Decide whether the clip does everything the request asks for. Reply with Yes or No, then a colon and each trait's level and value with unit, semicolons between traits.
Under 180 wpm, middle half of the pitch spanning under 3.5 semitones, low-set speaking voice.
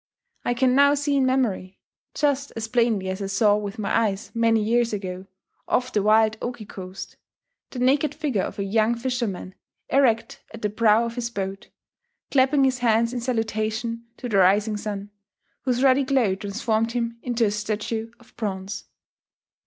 No: average, 170 wpm; average, 3.1 semitones; high, 225 Hz